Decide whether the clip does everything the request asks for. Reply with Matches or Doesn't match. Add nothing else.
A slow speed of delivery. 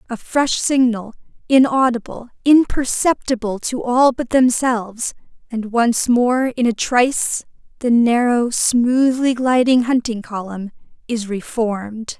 Matches